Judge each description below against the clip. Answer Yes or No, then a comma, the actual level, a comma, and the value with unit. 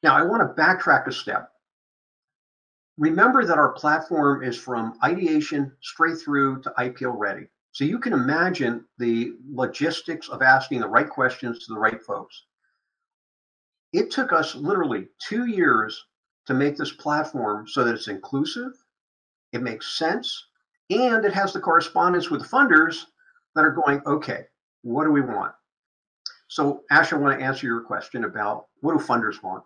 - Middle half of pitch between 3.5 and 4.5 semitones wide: No, wide, 5.5 semitones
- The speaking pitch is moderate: Yes, medium, 145 Hz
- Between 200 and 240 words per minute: No, average, 160 wpm